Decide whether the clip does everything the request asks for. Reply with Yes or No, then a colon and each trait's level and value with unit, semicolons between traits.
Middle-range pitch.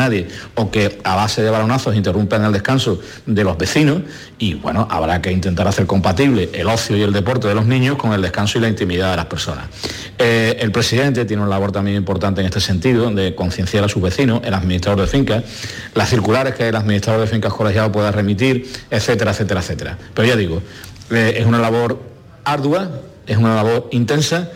No: low, 110 Hz